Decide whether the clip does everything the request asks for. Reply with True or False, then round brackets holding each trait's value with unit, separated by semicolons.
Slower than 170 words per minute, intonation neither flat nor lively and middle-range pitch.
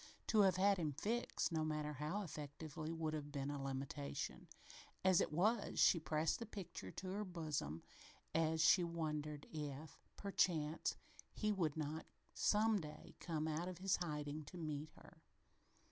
True (160 wpm; 3.5 semitones; 160 Hz)